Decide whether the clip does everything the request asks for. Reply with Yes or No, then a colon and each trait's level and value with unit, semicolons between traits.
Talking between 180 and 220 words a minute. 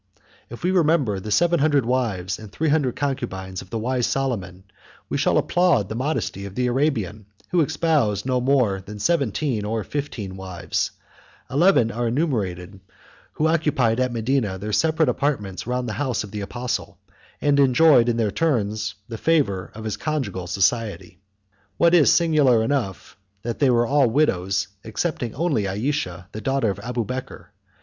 No: average, 160 wpm